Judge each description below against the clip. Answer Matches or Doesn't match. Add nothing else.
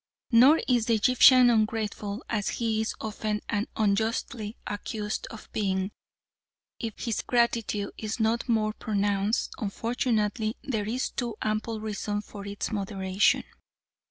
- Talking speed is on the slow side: Matches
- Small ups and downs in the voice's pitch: Matches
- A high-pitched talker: Matches